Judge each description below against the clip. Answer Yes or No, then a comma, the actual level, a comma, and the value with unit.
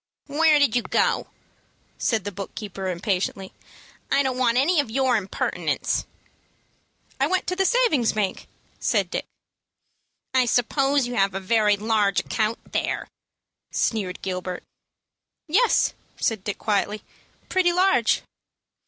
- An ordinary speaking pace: No, slow, 130 wpm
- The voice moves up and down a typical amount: No, wide, 5.8 semitones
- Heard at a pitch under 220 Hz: No, high, 230 Hz